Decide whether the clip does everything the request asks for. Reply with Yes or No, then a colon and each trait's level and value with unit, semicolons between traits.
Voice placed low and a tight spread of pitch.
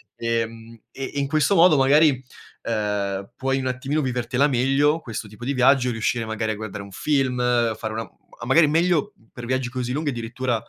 No: low, 125 Hz; average, 3.5 semitones